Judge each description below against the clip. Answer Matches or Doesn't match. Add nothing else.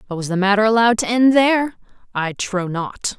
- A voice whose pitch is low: Doesn't match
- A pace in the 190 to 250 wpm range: Matches